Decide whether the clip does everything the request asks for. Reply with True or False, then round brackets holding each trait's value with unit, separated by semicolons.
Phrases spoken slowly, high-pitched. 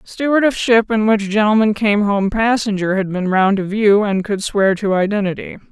False (200 wpm; 205 Hz)